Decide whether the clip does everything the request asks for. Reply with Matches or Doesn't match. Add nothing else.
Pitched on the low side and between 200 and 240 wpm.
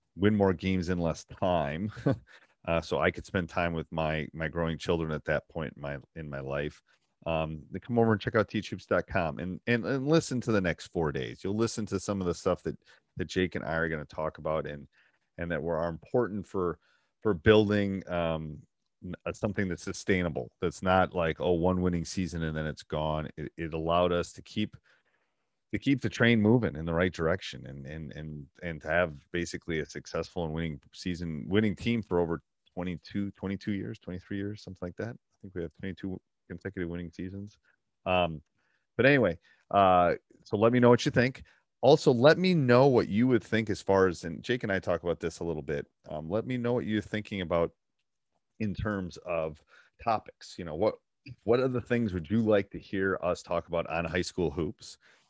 Matches